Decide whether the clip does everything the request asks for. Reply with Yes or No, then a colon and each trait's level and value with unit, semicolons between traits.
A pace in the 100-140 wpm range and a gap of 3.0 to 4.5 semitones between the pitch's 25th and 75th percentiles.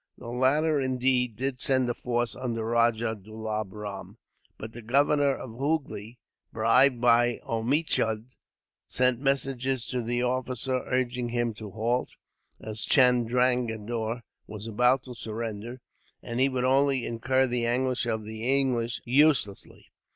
No: slow, 135 wpm; narrow, 2.4 semitones